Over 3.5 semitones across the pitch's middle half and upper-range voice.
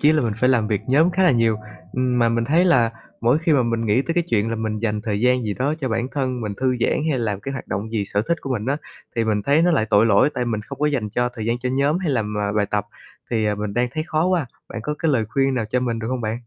No: average, 4.2 semitones; low, 120 Hz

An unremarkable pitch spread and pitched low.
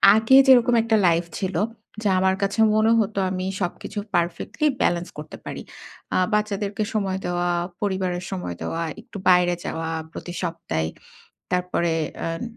No: average, 3.2 semitones; medium, 185 Hz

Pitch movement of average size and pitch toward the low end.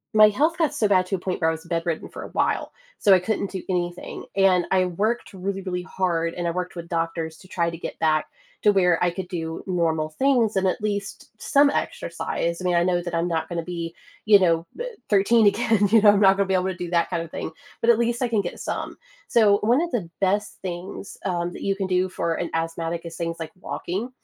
No: average, 3.2 semitones; medium, 185 Hz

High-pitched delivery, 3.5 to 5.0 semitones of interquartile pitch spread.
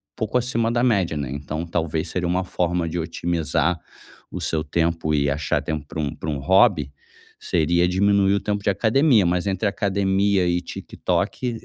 No: very low, 90 Hz; average, 3.9 semitones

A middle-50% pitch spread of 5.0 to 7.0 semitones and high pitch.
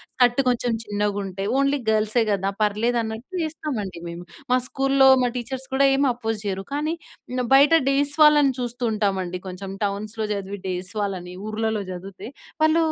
Yes: average, 5.3 semitones; high, 220 Hz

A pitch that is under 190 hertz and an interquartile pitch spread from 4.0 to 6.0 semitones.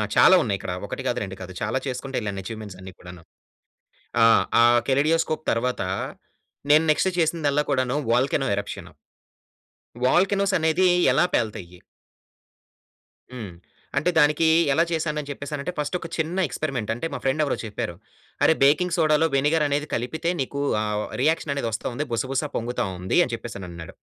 Yes: low, 135 Hz; wide, 5.6 semitones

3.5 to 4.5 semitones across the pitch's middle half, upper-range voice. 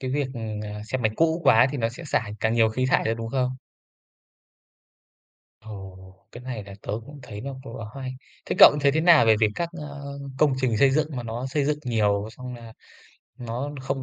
No: average, 3.9 semitones; low, 125 Hz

